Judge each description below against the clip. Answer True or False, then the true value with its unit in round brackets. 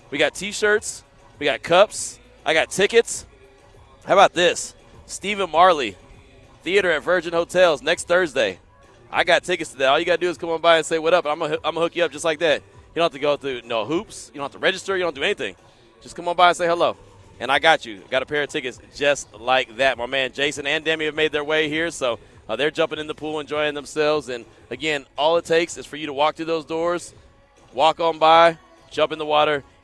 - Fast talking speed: True (250 wpm)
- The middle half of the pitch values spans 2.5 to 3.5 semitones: True (2.9 semitones)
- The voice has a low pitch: False (155 Hz)